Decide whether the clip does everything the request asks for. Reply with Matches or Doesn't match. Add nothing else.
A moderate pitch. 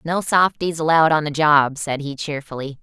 Matches